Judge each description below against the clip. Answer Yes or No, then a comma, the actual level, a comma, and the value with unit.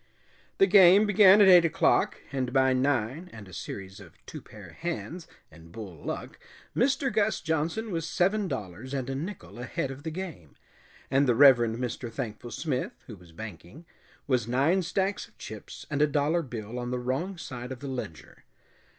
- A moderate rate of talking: Yes, average, 180 wpm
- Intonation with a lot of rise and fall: Yes, wide, 6.6 semitones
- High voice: No, low, 135 Hz